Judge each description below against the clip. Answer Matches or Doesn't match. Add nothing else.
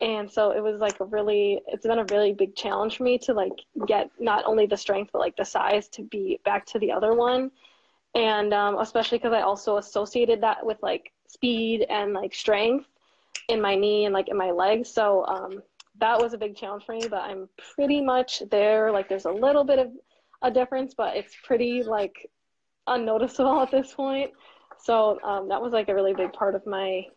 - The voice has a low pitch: Doesn't match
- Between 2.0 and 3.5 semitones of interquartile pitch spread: Matches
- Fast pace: Matches